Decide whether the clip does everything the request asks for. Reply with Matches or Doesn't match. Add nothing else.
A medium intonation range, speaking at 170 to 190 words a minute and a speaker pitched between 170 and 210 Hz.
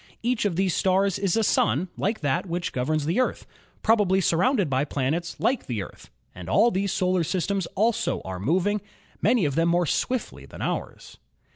Matches